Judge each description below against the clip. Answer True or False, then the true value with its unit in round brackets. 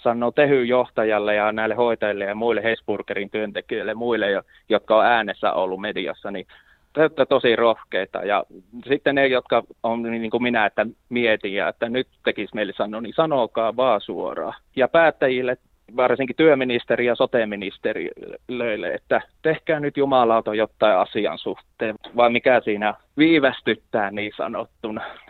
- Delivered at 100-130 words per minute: False (140 wpm)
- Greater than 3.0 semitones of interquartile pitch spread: True (3.4 semitones)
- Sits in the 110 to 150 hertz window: True (120 Hz)